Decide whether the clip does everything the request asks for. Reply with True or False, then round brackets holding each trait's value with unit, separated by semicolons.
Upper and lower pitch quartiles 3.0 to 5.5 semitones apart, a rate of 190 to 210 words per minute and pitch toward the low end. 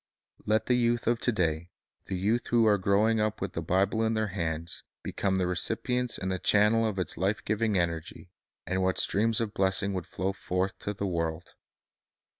True (3.3 semitones; 195 wpm; 100 Hz)